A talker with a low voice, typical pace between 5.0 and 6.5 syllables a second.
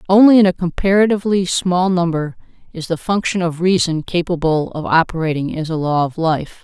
No: medium, 175 Hz; 5.4 syllables/s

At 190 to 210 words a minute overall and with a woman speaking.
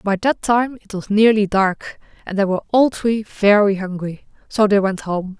Yes: average, 200 wpm; female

